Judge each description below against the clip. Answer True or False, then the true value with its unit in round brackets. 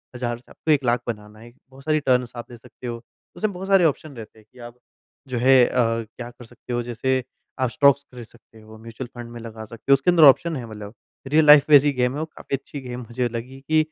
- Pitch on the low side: True (125 Hz)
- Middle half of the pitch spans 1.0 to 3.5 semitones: True (3.2 semitones)